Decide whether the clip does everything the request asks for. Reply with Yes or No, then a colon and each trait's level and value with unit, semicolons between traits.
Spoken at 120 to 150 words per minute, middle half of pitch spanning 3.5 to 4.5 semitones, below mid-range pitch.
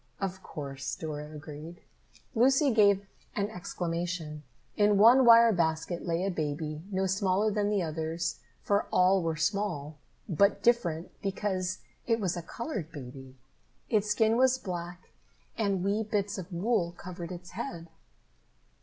No: average, 140 wpm; average, 4.1 semitones; medium, 185 Hz